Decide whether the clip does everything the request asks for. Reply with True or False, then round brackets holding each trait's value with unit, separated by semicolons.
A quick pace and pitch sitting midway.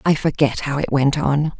True (225 wpm; 145 Hz)